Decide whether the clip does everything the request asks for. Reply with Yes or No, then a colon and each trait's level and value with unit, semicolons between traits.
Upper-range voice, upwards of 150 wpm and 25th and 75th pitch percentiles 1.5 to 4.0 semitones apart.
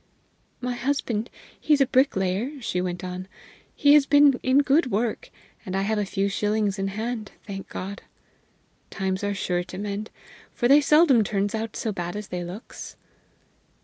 No: high, 210 Hz; average, 170 wpm; average, 5.0 semitones